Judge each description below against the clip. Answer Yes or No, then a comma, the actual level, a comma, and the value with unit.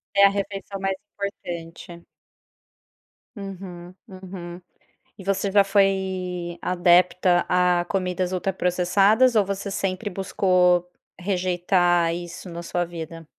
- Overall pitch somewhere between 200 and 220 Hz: No, medium, 185 Hz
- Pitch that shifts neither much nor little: No, narrow, 1.8 semitones